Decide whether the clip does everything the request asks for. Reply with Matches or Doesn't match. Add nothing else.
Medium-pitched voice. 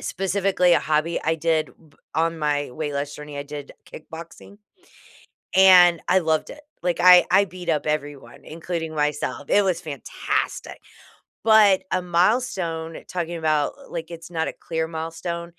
Matches